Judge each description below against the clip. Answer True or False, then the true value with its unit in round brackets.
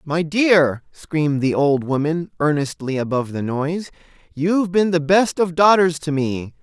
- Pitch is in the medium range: True (160 Hz)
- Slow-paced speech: False (165 wpm)